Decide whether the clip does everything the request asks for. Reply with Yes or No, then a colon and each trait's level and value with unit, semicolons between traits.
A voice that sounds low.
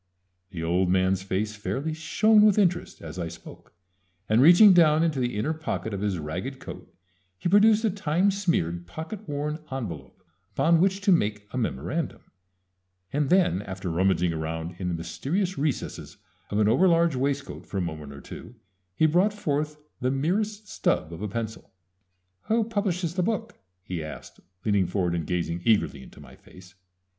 Yes: low, 130 Hz